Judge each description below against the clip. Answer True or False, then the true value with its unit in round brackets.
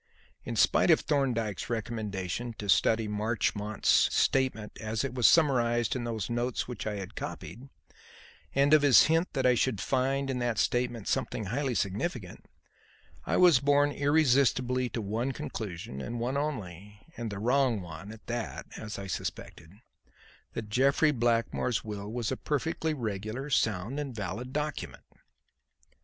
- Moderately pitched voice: False (120 Hz)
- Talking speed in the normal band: True (150 wpm)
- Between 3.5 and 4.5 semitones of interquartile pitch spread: True (4.1 semitones)